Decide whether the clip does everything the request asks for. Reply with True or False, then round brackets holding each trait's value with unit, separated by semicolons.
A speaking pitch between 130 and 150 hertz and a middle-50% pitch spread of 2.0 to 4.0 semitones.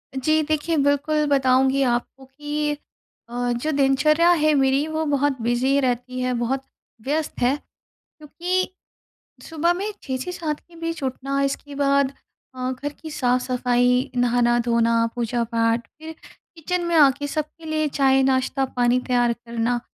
False (270 Hz; 3.6 semitones)